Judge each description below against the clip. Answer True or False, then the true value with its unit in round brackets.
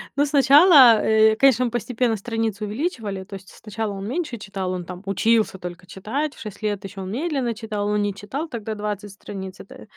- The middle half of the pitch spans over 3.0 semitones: True (3.6 semitones)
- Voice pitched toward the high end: True (215 Hz)